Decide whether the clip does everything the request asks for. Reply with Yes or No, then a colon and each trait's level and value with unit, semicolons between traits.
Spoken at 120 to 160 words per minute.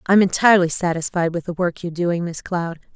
No: fast, 205 wpm